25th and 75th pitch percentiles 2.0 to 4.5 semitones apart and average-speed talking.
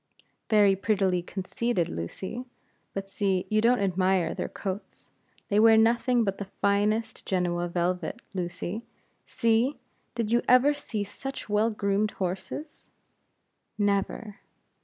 No: average, 3.2 semitones; slow, 120 wpm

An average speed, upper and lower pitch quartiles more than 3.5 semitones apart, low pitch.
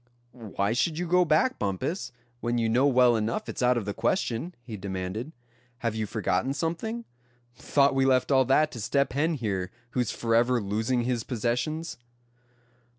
Yes: average, 165 wpm; average, 4.1 semitones; low, 125 Hz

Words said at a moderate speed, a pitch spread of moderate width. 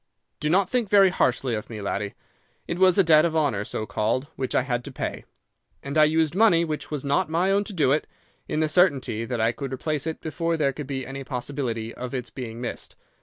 No: fast, 230 wpm; average, 5.0 semitones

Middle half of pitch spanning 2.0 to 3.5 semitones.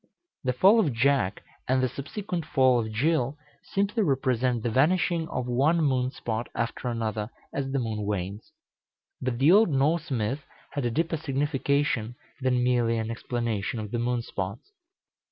No: average, 4.0 semitones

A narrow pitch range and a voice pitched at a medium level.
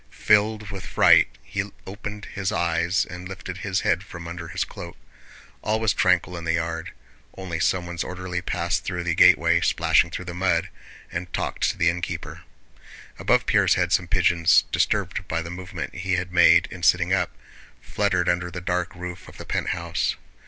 No: narrow, 1.5 semitones; very low, 90 Hz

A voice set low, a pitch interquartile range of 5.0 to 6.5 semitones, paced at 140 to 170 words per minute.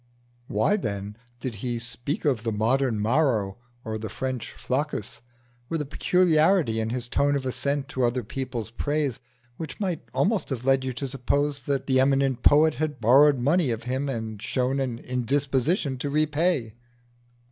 No: low, 130 Hz; average, 3.5 semitones; average, 165 wpm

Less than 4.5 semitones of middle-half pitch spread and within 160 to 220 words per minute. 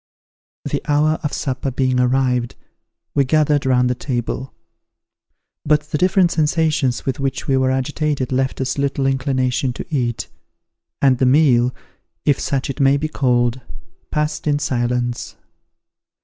No: narrow, 2.6 semitones; average, 140 wpm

